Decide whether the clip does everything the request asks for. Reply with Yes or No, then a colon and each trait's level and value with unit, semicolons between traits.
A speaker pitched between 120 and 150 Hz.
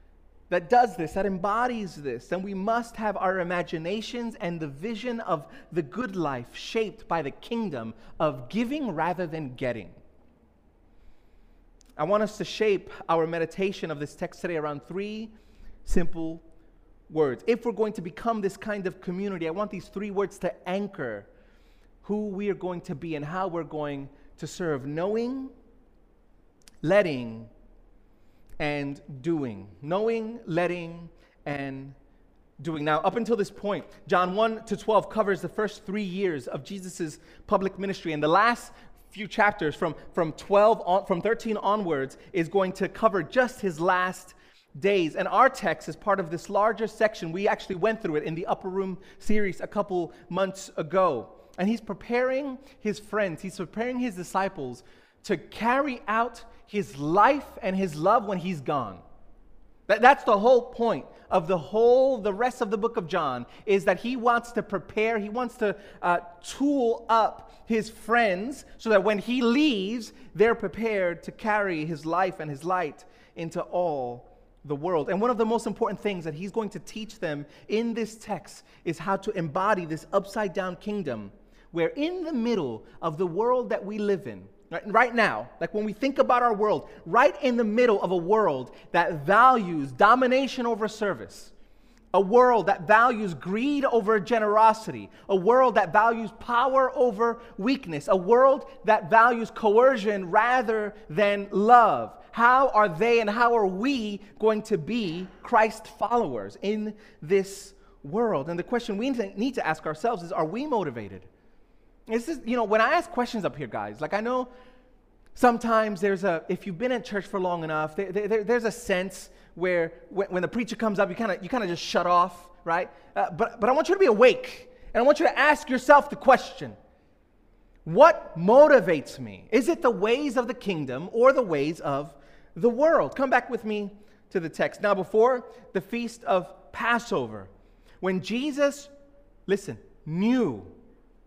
No: high, 205 Hz